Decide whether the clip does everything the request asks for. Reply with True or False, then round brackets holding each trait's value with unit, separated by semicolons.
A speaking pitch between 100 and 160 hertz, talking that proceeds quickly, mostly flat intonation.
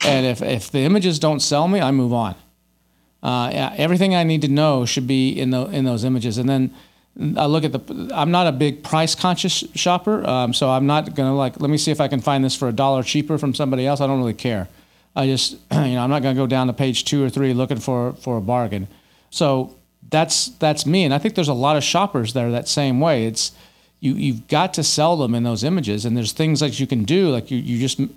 False (135 Hz; 260 wpm; 3.5 semitones)